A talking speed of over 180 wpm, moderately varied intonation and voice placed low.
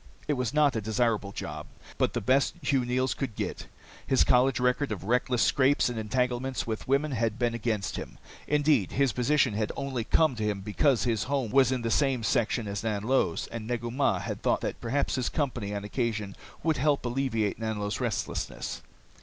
Yes: average, 190 wpm; average, 3.5 semitones; low, 120 Hz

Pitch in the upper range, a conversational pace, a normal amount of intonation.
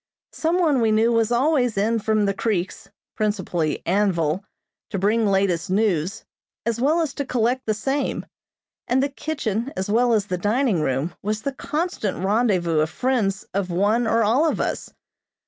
Yes: high, 215 Hz; average, 170 wpm; average, 4.2 semitones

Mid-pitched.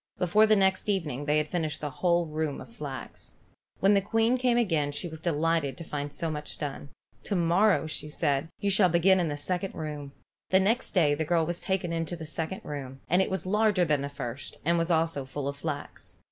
Yes: medium, 165 Hz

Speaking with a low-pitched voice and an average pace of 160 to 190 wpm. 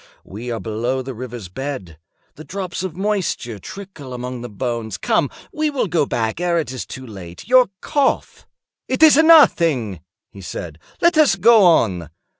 Yes: low, 130 Hz; average, 170 wpm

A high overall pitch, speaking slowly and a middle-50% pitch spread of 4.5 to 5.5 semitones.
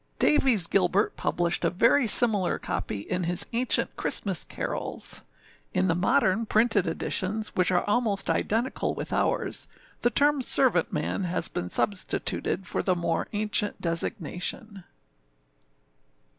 No: high, 200 Hz; slow, 125 wpm; average, 4.1 semitones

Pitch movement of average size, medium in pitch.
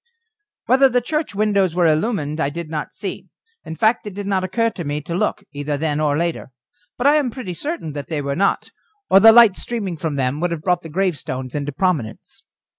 No: wide, 6.2 semitones; medium, 175 Hz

